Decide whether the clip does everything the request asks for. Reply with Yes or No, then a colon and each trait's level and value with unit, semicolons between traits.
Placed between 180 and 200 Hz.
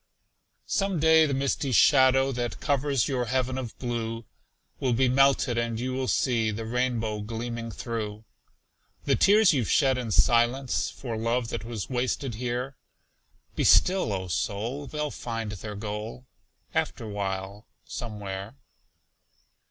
No: low, 120 Hz